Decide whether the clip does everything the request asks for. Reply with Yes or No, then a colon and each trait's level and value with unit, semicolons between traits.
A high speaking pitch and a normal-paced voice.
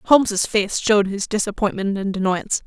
Yes: high, 205 Hz; average, 160 wpm